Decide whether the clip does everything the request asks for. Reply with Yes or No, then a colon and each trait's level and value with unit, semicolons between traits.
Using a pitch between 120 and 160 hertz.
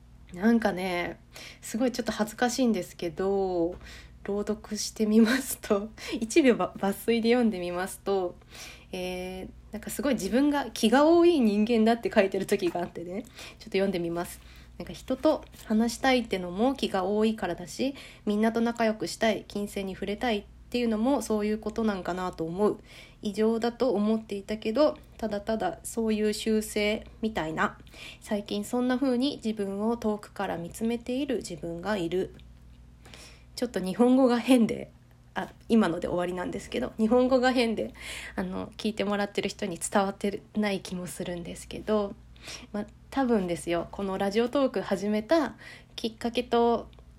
No: high, 210 Hz